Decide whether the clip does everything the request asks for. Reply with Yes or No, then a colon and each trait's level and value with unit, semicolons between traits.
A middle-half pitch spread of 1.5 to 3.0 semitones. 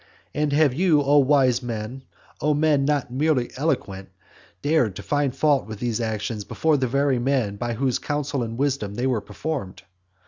No: average, 3.9 semitones